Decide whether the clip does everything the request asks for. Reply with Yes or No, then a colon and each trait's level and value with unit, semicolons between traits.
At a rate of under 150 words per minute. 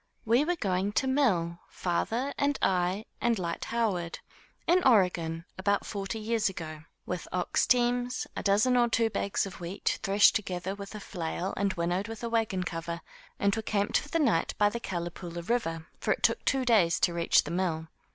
No: average, 185 wpm